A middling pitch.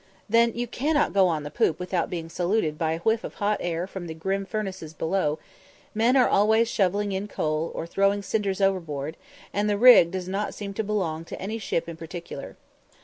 No: high, 195 Hz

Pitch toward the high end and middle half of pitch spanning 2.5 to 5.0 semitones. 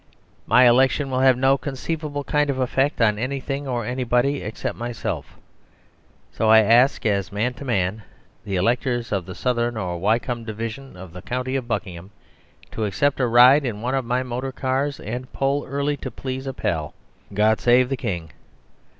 No: low, 125 Hz; average, 3.5 semitones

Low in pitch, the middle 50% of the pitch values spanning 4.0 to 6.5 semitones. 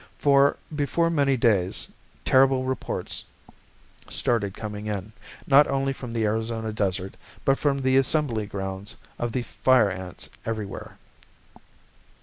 Yes: low, 115 Hz; average, 4.6 semitones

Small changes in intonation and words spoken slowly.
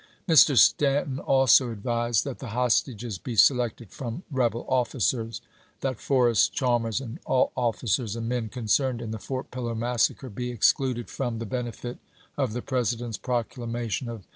No: narrow, 2.1 semitones; average, 155 wpm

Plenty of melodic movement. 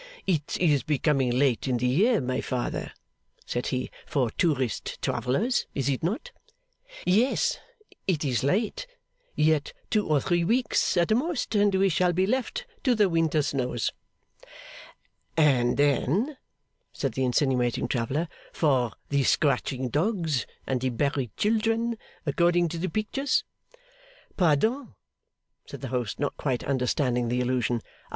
Yes: wide, 7.3 semitones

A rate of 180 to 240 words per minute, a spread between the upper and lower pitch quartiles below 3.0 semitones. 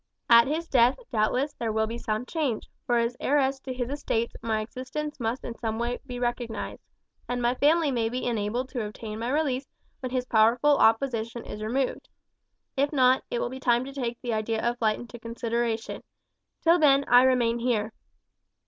Yes: average, 185 wpm; narrow, 2.5 semitones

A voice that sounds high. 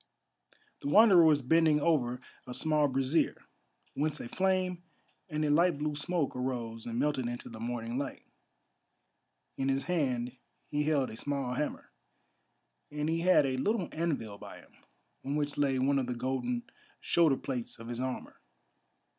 No: medium, 140 Hz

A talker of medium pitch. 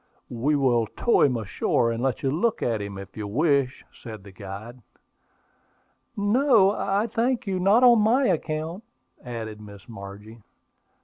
No: low, 130 Hz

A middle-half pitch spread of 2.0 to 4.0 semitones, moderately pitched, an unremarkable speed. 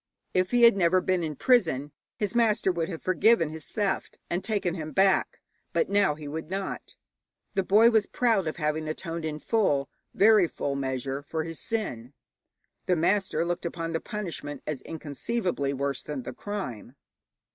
No: average, 5.0 semitones; medium, 170 Hz; average, 170 wpm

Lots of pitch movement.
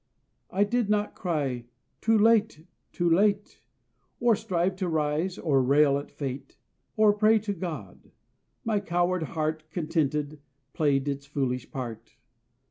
Yes: wide, 6.0 semitones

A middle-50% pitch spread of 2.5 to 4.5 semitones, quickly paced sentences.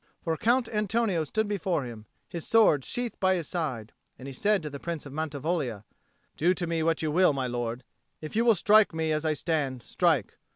No: average, 5.2 semitones; fast, 210 wpm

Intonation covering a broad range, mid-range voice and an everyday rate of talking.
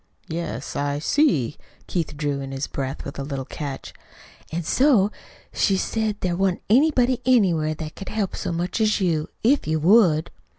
Yes: wide, 6.5 semitones; medium, 170 Hz; average, 170 wpm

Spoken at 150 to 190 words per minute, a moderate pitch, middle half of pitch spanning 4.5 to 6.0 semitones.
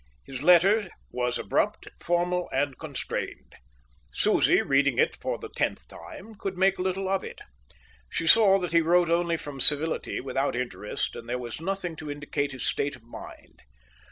Yes: average, 165 wpm; medium, 160 Hz; average, 4.8 semitones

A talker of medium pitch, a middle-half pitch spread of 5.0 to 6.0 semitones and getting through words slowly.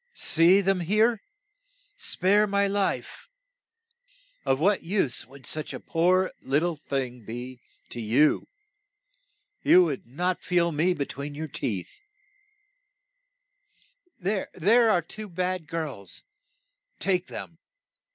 Yes: medium, 170 Hz; average, 5.3 semitones; slow, 115 wpm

